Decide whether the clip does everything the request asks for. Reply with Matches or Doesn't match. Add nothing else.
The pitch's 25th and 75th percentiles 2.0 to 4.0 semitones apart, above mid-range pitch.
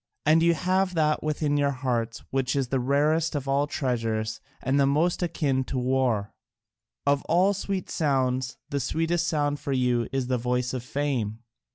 Doesn't match